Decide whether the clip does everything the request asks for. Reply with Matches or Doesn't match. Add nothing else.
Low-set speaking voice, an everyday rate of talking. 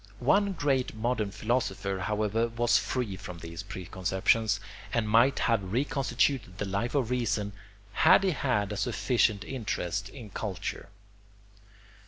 Doesn't match